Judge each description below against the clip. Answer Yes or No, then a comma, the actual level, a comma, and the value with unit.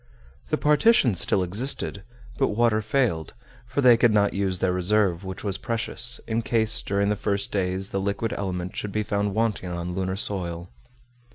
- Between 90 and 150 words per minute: No, average, 175 wpm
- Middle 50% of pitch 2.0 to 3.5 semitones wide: Yes, average, 3.2 semitones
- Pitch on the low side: Yes, low, 100 Hz